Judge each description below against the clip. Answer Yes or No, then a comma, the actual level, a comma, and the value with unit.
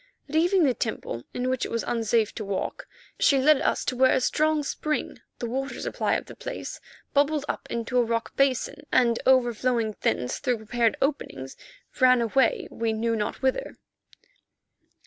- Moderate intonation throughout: Yes, average, 3.3 semitones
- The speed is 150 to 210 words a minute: Yes, average, 165 wpm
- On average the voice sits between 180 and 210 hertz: No, very high, 250 Hz